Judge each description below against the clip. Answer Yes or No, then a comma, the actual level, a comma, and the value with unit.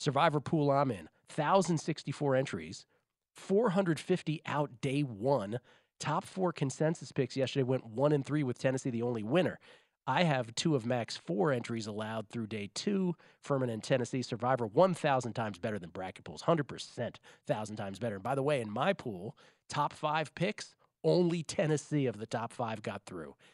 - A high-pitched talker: No, medium, 140 Hz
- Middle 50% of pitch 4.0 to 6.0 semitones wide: Yes, average, 4.7 semitones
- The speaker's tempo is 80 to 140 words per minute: No, average, 185 wpm